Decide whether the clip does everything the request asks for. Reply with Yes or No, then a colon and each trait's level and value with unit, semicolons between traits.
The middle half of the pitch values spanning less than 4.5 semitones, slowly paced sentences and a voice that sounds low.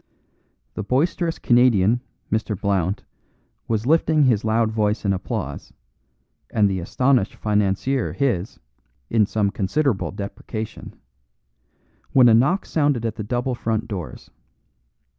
Yes: average, 3.9 semitones; slow, 120 wpm; low, 110 Hz